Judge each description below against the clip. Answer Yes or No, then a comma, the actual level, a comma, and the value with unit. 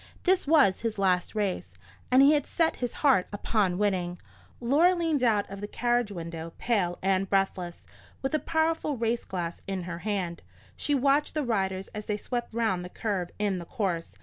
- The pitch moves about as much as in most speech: No, wide, 5.9 semitones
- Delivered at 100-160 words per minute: No, average, 185 wpm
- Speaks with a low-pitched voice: No, high, 210 Hz